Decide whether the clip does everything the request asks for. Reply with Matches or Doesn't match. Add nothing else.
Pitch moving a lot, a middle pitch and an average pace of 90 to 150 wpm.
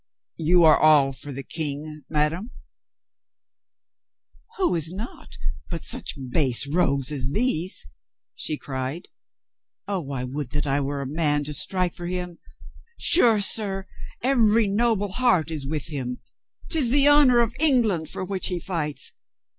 Matches